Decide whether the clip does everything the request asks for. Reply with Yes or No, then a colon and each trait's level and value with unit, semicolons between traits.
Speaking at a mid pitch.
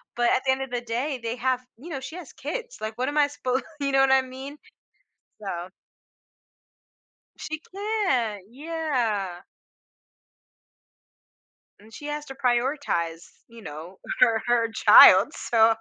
No: very high, 255 Hz